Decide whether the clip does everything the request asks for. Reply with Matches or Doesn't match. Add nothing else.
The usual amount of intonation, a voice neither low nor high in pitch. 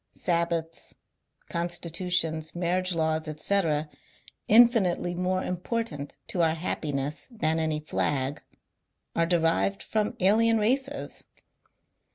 Matches